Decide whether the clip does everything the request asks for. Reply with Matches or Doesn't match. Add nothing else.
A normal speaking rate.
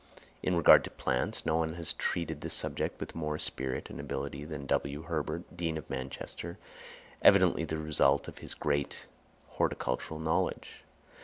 Matches